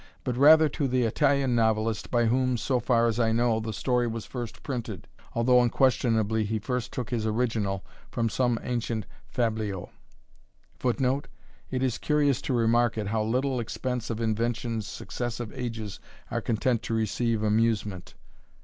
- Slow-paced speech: No, average, 155 wpm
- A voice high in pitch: No, low, 115 Hz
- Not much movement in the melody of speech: Yes, narrow, 2.1 semitones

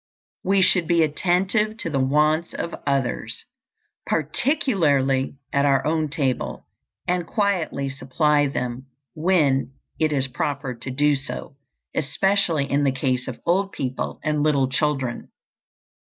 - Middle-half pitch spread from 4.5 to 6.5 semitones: No, average, 4.1 semitones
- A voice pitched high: No, medium, 145 Hz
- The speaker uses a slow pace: Yes, slow, 130 wpm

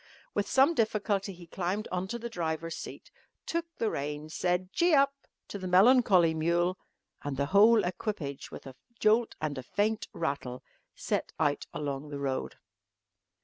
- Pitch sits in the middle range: Yes, medium, 180 Hz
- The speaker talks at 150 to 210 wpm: Yes, average, 155 wpm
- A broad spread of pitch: Yes, wide, 6.0 semitones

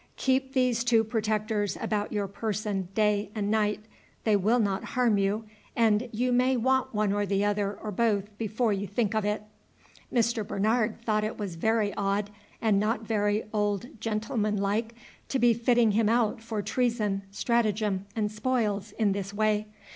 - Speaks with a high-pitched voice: Yes, high, 215 Hz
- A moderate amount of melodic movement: No, narrow, 1.9 semitones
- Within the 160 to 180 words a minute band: Yes, average, 165 wpm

